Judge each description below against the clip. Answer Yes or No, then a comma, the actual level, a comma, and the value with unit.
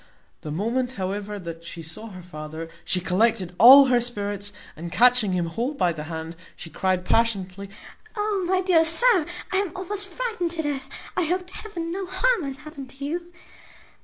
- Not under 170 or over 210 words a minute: Yes, average, 185 wpm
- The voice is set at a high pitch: Yes, high, 245 Hz